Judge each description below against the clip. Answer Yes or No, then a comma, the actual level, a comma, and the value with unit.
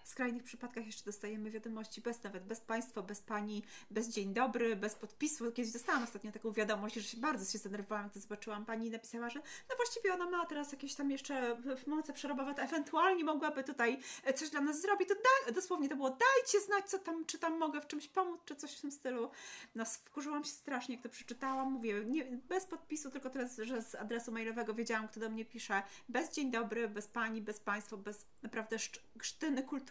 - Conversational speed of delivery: No, fast, 210 wpm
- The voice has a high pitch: Yes, high, 245 Hz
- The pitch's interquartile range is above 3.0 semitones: Yes, average, 5.1 semitones